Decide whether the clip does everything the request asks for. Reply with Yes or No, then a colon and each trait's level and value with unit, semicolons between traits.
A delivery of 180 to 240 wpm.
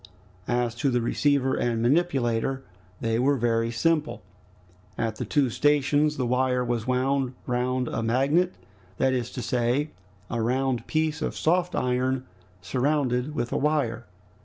No: average, 145 wpm